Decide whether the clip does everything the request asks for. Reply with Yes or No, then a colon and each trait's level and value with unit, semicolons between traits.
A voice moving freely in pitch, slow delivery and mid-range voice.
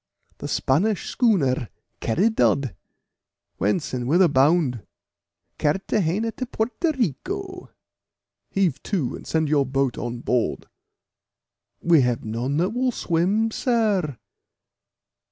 Yes: wide, 8.7 semitones; slow, 105 wpm; medium, 165 Hz